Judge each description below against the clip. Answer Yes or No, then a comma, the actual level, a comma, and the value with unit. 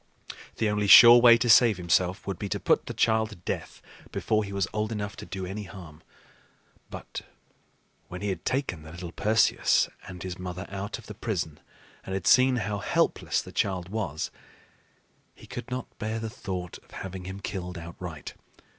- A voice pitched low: Yes, low, 100 Hz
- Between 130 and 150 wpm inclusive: No, average, 185 wpm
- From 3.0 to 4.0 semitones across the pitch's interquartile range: Yes, average, 3.3 semitones